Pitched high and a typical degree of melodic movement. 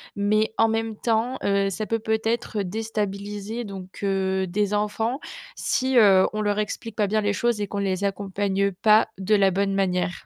No: high, 205 Hz; narrow, 2.0 semitones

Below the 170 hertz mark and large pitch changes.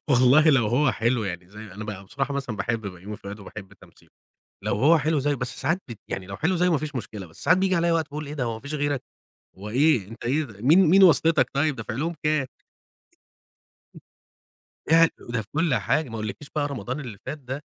Yes: low, 135 Hz; wide, 5.9 semitones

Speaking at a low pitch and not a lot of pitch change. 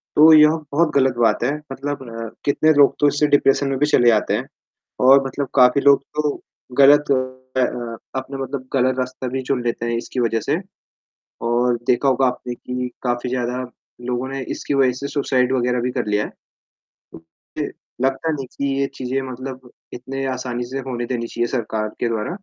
Yes: low, 130 Hz; narrow, 2.2 semitones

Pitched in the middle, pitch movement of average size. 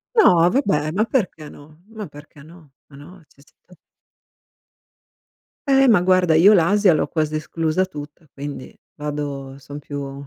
Yes: medium, 155 Hz; average, 4.0 semitones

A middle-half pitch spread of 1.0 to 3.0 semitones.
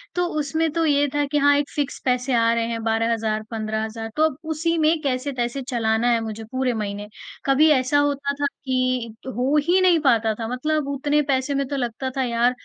No: average, 4.0 semitones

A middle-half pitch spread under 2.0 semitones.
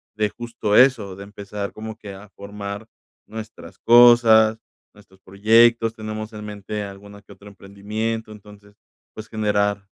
Yes: narrow, 1.6 semitones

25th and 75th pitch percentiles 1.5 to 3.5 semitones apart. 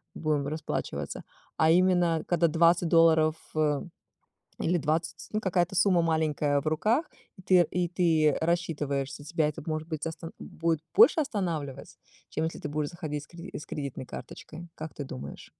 Yes: narrow, 2.5 semitones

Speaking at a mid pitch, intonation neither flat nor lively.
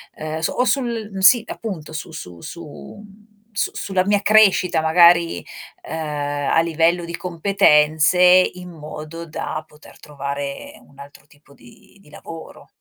Yes: medium, 165 Hz; average, 4.1 semitones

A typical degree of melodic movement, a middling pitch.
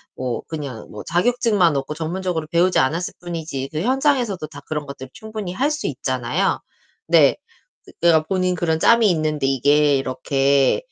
Yes: average, 4.9 semitones; medium, 160 Hz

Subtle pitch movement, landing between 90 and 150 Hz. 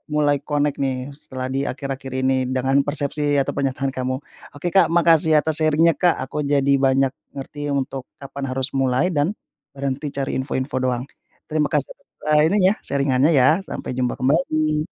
Yes: narrow, 2.3 semitones; medium, 140 Hz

